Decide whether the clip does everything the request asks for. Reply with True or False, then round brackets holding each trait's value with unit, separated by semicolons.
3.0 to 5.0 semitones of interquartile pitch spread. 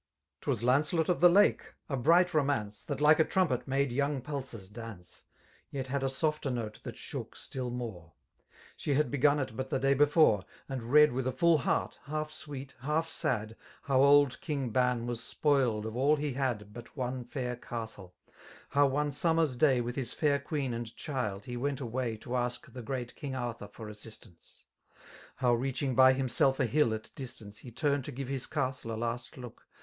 True (3.3 semitones)